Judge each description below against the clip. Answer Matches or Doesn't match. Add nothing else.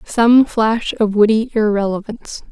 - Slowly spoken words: Matches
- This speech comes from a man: Doesn't match